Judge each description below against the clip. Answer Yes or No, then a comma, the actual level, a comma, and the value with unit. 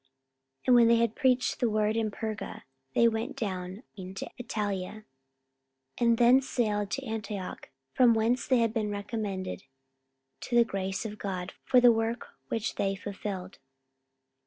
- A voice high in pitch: Yes, high, 220 Hz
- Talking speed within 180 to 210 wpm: No, average, 160 wpm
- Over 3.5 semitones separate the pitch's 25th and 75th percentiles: No, average, 2.8 semitones